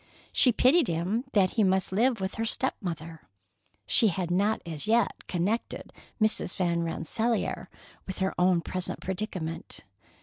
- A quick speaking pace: No, average, 145 wpm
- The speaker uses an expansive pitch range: No, average, 4.4 semitones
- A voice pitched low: No, high, 190 Hz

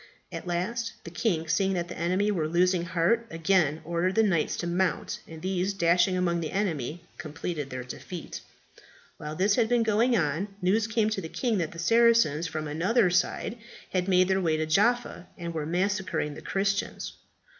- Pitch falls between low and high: Yes, medium, 180 Hz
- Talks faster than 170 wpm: Yes, average, 185 wpm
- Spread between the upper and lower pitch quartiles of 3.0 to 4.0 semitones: Yes, average, 3.5 semitones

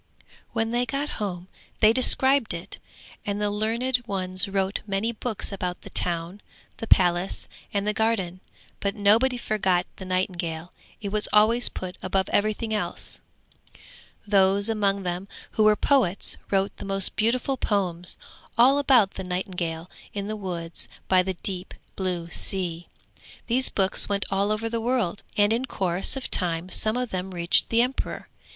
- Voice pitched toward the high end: Yes, high, 200 Hz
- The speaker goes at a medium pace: Yes, average, 160 wpm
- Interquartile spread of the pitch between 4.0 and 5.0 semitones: No, average, 3.5 semitones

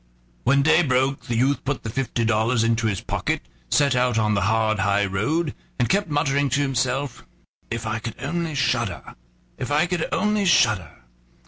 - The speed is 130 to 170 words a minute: No, average, 180 wpm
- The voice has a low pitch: Yes, low, 125 Hz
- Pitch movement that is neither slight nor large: Yes, average, 4.4 semitones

